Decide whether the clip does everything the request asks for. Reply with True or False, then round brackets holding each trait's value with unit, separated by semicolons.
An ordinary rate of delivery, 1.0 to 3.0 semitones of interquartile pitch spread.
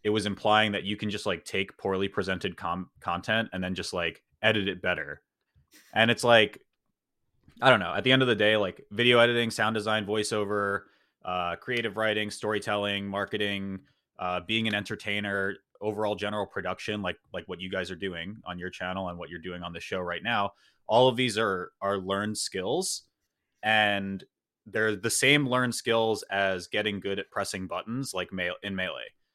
True (190 wpm; 2.4 semitones)